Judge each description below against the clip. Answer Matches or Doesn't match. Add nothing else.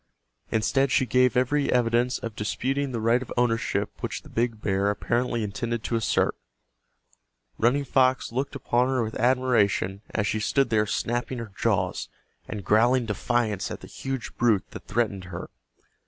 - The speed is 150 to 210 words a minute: Matches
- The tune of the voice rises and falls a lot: Doesn't match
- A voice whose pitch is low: Matches